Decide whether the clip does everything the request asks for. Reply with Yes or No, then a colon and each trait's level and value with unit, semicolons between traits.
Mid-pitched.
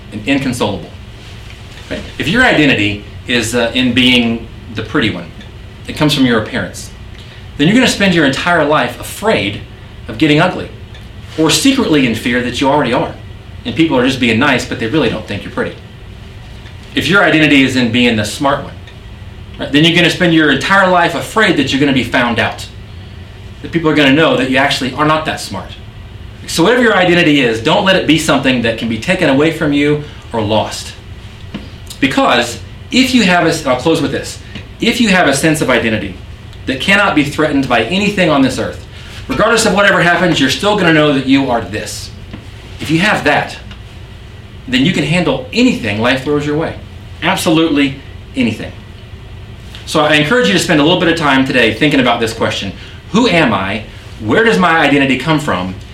No: low, 120 Hz